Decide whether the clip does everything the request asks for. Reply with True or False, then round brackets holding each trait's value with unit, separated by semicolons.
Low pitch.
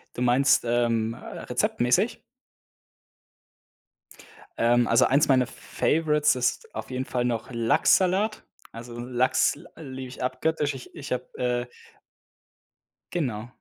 True (125 Hz)